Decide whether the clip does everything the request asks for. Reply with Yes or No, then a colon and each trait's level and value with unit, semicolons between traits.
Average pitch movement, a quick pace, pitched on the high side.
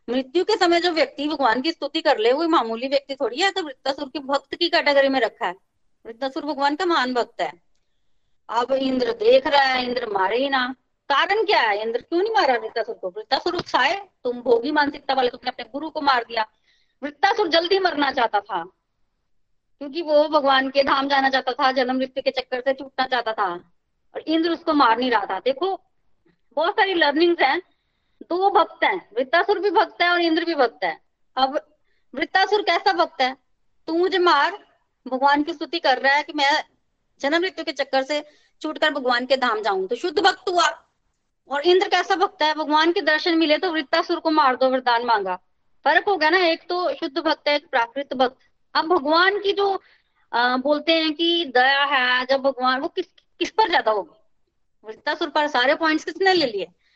Yes: average, 4.8 semitones; fast, 200 wpm; very high, 300 Hz